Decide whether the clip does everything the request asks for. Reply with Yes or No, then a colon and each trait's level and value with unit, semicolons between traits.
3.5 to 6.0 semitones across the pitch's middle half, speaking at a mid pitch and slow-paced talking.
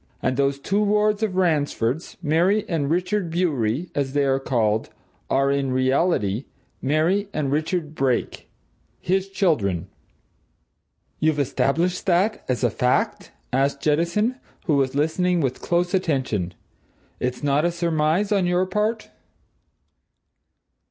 Yes: average, 5.1 semitones; medium, 155 Hz; slow, 125 wpm